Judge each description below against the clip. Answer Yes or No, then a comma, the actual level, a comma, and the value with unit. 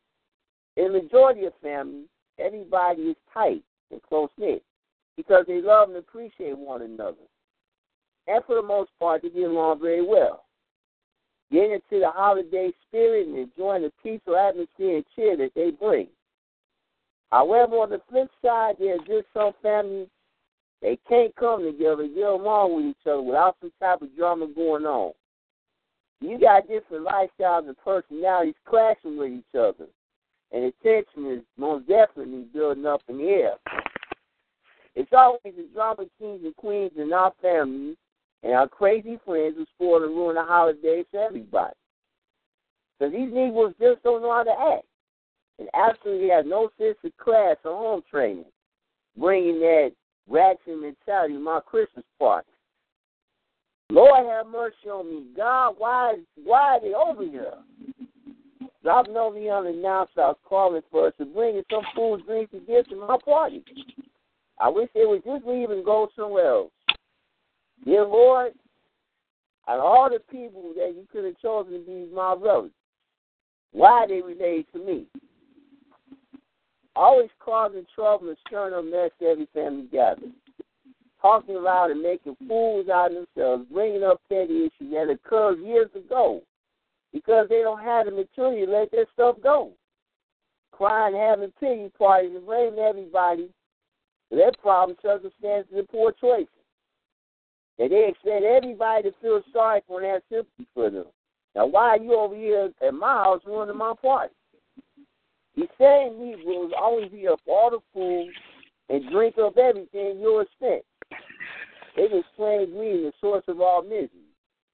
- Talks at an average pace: Yes, average, 160 wpm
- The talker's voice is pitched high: Yes, high, 210 Hz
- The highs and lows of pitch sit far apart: Yes, wide, 6.2 semitones